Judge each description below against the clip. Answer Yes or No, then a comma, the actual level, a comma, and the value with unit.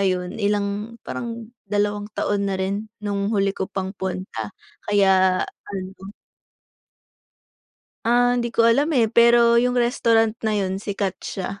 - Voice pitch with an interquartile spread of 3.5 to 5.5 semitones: No, average, 3.1 semitones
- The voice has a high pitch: Yes, high, 205 Hz